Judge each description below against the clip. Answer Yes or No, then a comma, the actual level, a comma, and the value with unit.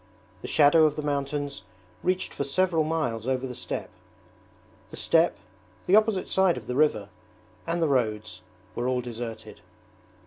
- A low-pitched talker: No, medium, 145 Hz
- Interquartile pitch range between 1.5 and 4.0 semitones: No, average, 4.8 semitones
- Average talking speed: Yes, average, 150 wpm